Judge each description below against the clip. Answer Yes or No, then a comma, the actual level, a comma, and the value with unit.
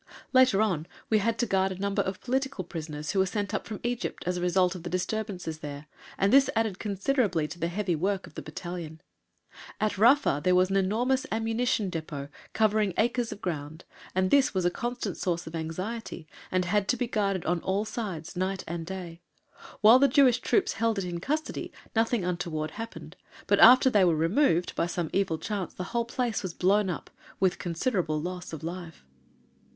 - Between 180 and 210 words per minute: Yes, average, 195 wpm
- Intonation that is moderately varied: Yes, average, 4.5 semitones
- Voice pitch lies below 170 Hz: No, high, 190 Hz